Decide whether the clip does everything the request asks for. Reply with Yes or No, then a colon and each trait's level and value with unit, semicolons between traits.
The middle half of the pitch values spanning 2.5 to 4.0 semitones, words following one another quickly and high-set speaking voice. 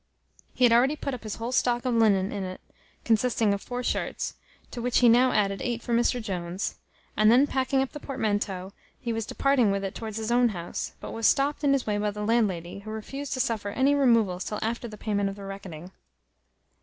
Yes: average, 3.7 semitones; fast, 220 wpm; high, 225 Hz